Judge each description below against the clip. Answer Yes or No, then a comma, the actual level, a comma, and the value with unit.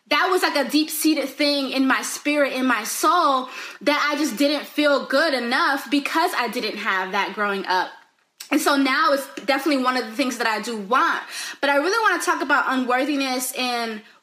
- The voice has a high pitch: Yes, very high, 270 Hz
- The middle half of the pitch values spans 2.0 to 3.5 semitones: Yes, average, 3.2 semitones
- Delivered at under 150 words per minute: No, average, 200 wpm